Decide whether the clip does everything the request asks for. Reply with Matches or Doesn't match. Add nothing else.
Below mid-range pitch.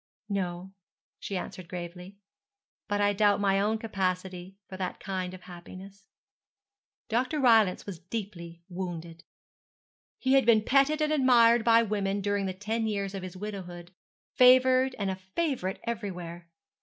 Doesn't match